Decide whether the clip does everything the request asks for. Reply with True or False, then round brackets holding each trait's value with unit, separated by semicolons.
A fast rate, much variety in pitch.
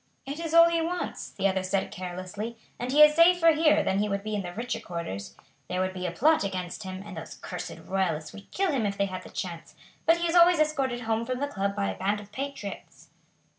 True (245 wpm; 8.2 semitones)